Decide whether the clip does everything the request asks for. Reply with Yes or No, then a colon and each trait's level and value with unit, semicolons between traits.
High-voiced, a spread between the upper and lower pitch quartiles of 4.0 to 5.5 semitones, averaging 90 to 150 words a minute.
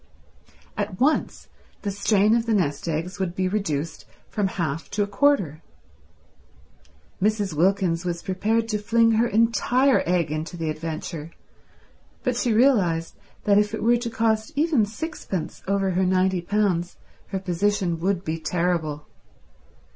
Yes: high, 195 Hz; average, 4.4 semitones; average, 145 wpm